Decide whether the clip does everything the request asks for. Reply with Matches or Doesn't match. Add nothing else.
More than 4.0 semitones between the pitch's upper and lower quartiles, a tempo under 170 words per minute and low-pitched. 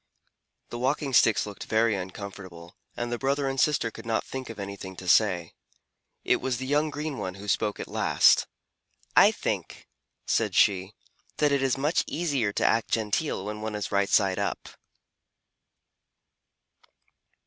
Matches